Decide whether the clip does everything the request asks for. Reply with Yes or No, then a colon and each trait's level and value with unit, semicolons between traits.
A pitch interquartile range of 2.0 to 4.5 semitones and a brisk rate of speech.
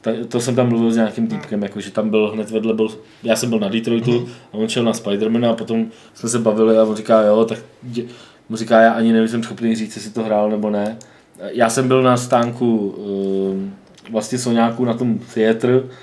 No: narrow, 1.6 semitones; fast, 215 wpm